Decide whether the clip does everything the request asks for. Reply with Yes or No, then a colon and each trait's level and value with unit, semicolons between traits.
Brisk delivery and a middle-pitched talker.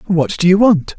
Yes: fast, 245 wpm; medium, 180 Hz